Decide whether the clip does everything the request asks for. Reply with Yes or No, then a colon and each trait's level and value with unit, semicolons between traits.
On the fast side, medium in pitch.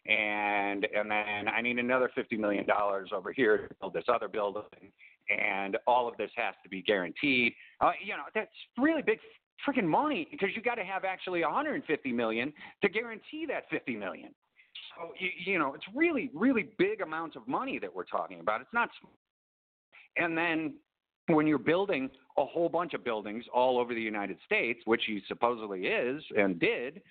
No: average, 185 wpm; medium, 145 Hz